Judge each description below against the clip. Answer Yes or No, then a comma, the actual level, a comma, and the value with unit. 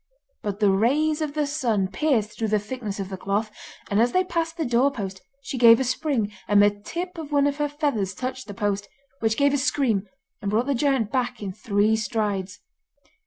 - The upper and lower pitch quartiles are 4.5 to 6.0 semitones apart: Yes, wide, 5.6 semitones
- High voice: Yes, high, 230 Hz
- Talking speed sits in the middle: No, fast, 210 wpm